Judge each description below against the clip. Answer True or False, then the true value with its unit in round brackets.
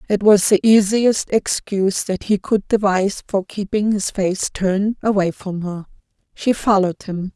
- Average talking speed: True (165 wpm)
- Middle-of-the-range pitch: False (200 Hz)